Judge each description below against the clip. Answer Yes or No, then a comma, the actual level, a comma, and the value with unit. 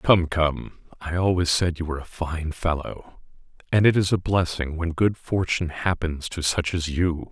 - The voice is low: Yes, very low, 85 Hz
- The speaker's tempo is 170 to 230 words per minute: Yes, average, 190 wpm